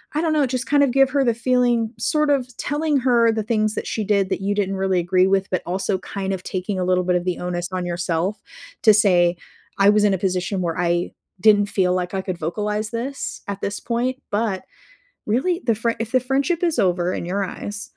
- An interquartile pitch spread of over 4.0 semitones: Yes, average, 4.8 semitones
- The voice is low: No, high, 205 Hz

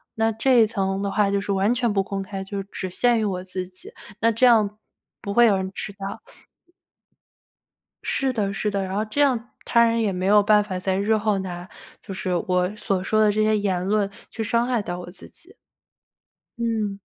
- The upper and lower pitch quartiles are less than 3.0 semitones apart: Yes, narrow, 2.5 semitones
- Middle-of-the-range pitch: No, high, 205 Hz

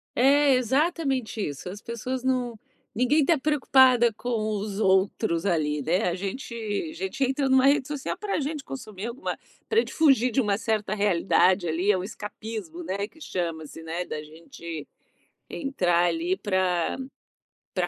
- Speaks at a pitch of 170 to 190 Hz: No, high, 220 Hz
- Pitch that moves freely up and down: Yes, wide, 6.5 semitones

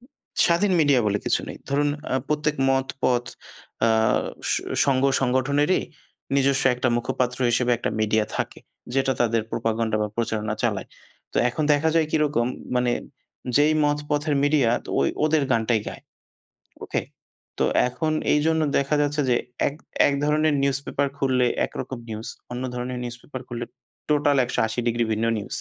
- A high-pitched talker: No, low, 130 Hz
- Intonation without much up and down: No, average, 3.6 semitones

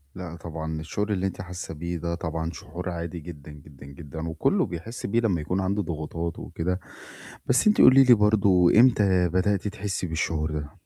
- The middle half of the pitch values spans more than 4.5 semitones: No, average, 3.5 semitones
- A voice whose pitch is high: No, very low, 85 Hz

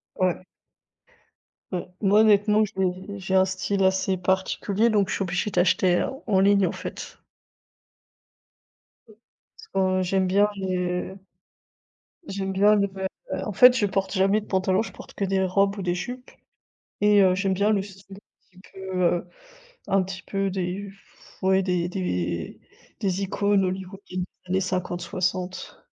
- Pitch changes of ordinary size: No, narrow, 1.4 semitones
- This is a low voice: No, high, 190 Hz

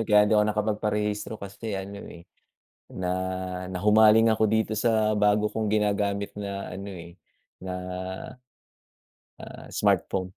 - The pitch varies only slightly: Yes, narrow, 1.4 semitones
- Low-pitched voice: Yes, low, 105 Hz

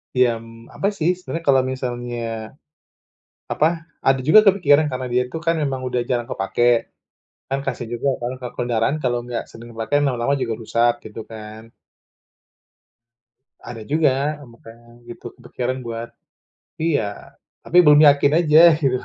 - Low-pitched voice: Yes, low, 125 Hz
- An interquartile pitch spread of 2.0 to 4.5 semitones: Yes, average, 3.5 semitones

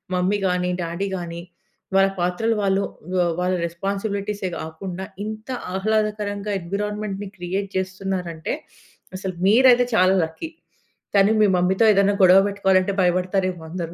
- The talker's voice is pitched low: No, high, 190 Hz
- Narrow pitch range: Yes, narrow, 2.1 semitones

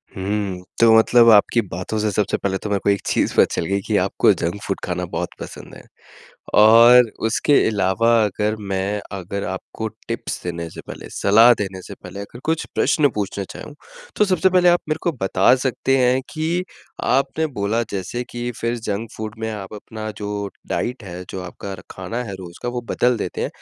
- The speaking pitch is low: Yes, low, 105 Hz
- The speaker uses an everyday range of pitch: Yes, average, 3.8 semitones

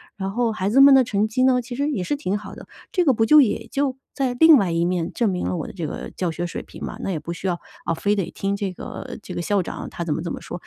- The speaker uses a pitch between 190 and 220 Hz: Yes, high, 200 Hz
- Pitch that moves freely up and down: Yes, wide, 6.4 semitones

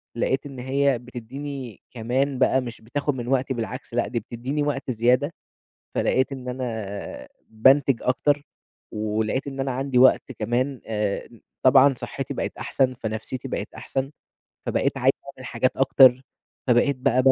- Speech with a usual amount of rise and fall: No, narrow, 2.3 semitones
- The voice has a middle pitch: No, low, 130 Hz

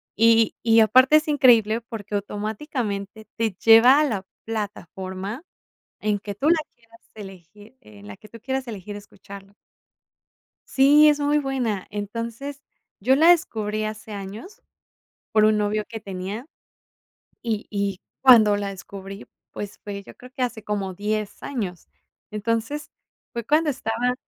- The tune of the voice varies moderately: Yes, average, 3.5 semitones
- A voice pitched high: Yes, high, 215 Hz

